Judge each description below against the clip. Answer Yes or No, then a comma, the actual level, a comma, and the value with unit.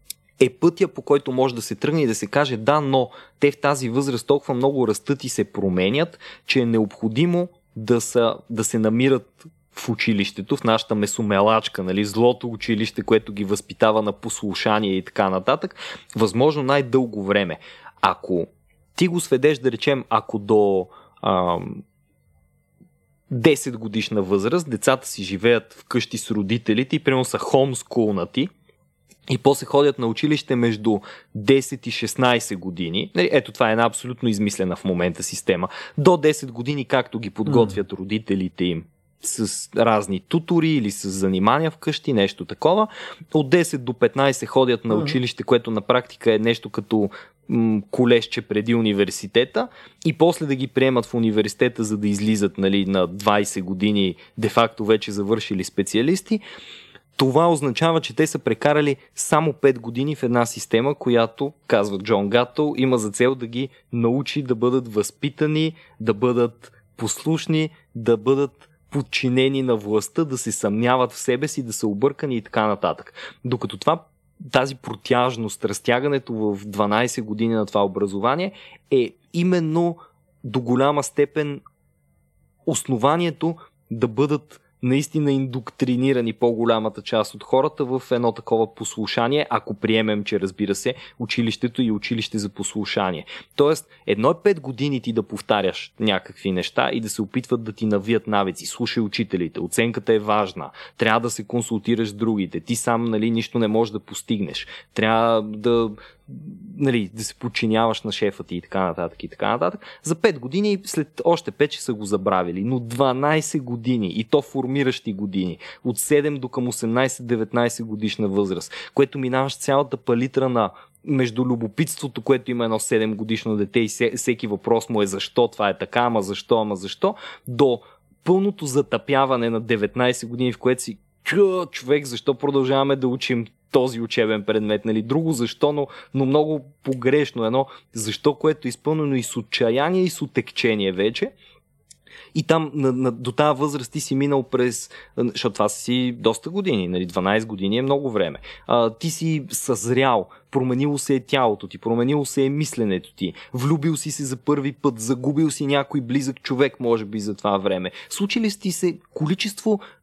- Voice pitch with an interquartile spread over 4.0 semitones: Yes, average, 4.5 semitones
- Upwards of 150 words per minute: Yes, average, 160 wpm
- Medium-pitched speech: No, low, 120 Hz